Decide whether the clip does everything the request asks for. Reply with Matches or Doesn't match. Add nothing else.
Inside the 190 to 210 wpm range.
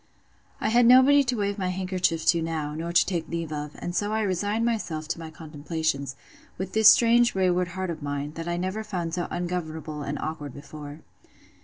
Matches